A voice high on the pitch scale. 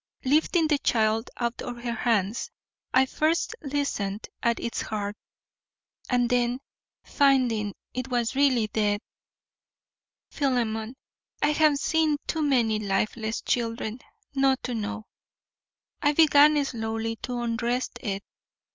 Yes: high, 240 Hz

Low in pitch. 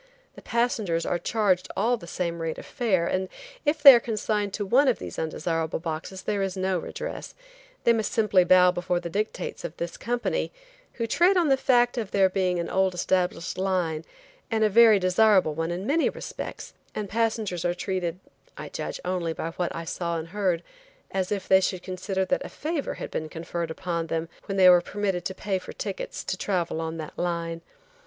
No: medium, 185 Hz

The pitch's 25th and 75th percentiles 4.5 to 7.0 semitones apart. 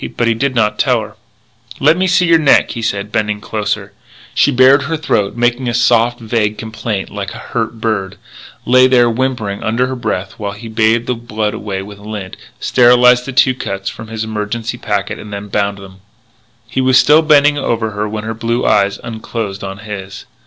No: average, 3.1 semitones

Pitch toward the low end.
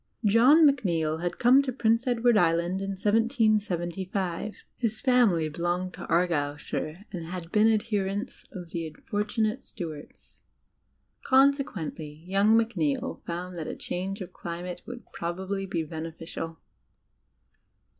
No: high, 190 Hz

